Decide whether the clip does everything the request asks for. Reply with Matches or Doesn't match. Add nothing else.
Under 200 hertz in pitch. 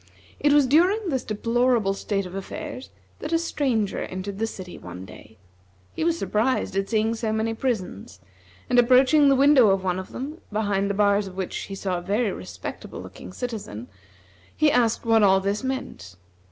Doesn't match